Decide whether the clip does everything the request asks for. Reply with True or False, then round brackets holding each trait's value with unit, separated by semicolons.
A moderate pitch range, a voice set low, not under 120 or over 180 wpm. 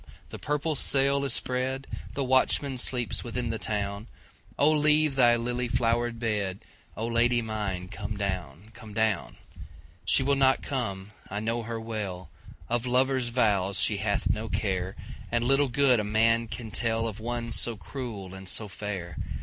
True (3.6 semitones; 115 Hz; 140 wpm)